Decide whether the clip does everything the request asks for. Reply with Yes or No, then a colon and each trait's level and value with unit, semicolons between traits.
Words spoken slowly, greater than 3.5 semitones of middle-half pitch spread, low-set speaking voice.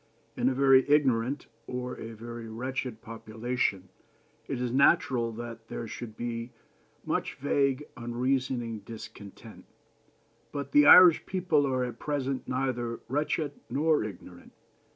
No: slow, 125 wpm; average, 3.1 semitones; low, 125 Hz